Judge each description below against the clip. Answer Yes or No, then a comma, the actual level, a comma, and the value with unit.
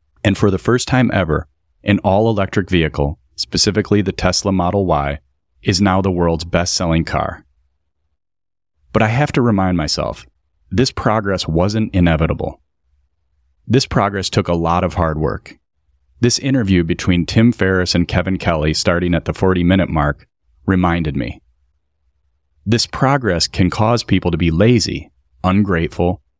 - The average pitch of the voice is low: Yes, very low, 90 Hz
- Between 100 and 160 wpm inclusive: Yes, average, 150 wpm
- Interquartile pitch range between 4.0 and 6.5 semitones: Yes, average, 4.7 semitones